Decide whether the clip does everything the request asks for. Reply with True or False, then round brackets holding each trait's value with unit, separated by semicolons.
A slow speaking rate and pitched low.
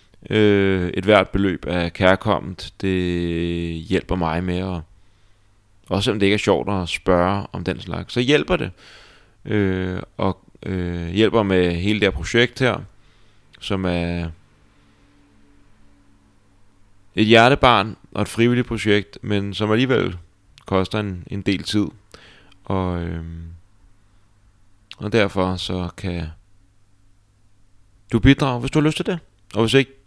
True (135 wpm; 100 Hz)